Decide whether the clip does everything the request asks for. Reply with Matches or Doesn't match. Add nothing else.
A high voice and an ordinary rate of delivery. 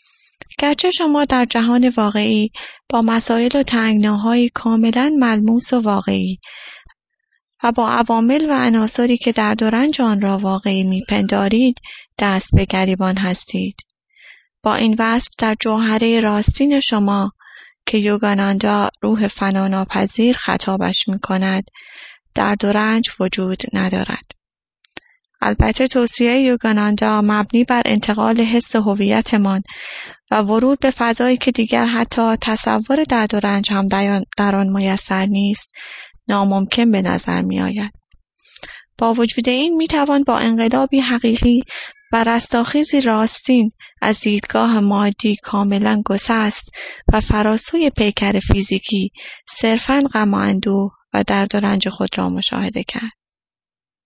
Doesn't match